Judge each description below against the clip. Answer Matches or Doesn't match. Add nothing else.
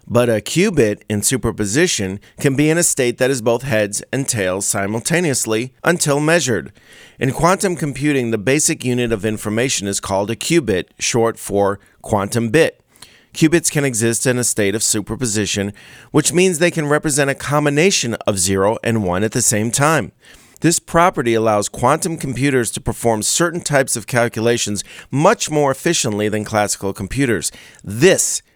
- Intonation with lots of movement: Matches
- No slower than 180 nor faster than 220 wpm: Doesn't match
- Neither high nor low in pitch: Doesn't match